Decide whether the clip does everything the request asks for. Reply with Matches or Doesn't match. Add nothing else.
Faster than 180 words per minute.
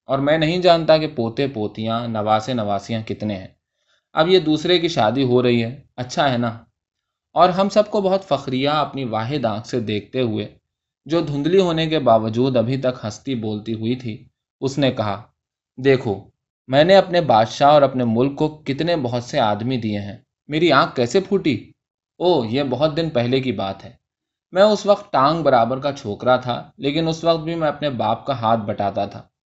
Matches